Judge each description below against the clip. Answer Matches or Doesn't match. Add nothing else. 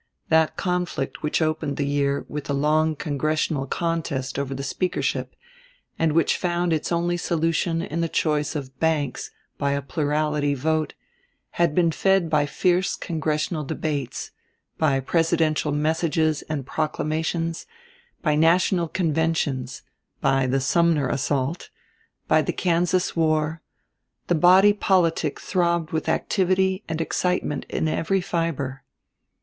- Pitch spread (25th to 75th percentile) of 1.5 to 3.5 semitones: Matches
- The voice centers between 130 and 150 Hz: Doesn't match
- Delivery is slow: Matches